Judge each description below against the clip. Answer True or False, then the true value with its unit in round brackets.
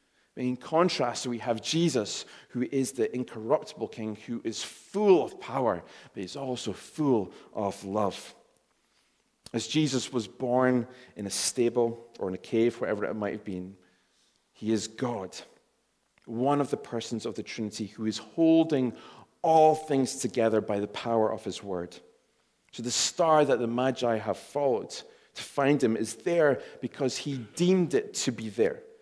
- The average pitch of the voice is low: True (120 Hz)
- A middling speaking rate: True (165 wpm)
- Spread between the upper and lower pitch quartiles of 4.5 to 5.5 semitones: False (3.8 semitones)